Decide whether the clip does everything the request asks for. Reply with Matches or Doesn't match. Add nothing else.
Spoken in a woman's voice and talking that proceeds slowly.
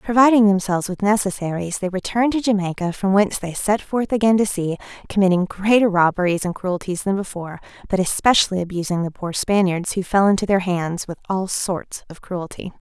Doesn't match